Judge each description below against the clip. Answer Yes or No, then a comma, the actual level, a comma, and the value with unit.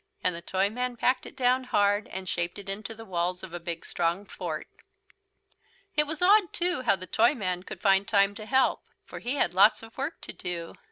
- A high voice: Yes, high, 205 Hz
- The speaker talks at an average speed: No, fast, 210 wpm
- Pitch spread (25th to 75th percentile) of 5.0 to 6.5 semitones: Yes, wide, 5.5 semitones